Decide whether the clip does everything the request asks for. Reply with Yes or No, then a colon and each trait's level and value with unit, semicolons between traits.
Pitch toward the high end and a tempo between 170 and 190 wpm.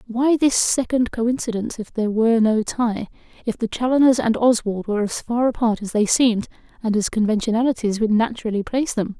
Yes: high, 225 Hz; average, 175 wpm